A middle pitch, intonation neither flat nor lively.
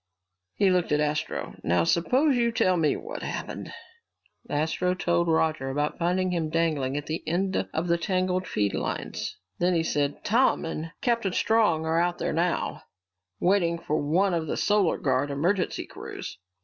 Yes: medium, 170 Hz; average, 3.2 semitones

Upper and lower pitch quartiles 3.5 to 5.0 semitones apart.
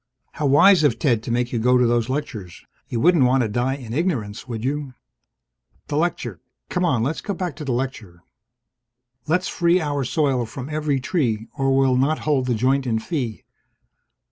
Yes: average, 4.0 semitones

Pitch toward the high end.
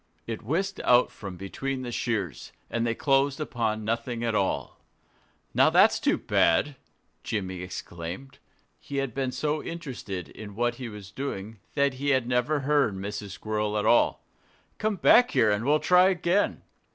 No: low, 120 Hz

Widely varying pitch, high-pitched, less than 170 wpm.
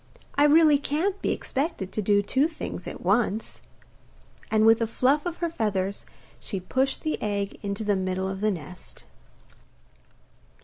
Yes: wide, 6.6 semitones; high, 220 Hz; average, 160 wpm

